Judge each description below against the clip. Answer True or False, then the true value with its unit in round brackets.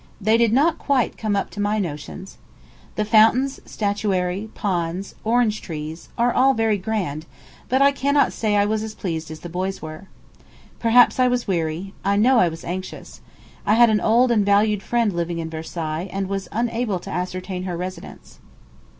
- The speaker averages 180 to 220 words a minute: True (185 wpm)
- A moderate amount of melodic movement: True (4.1 semitones)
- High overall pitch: True (205 Hz)